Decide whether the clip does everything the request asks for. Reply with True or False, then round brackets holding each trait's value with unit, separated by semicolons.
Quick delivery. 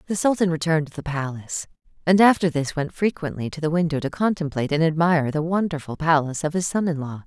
True (215 wpm)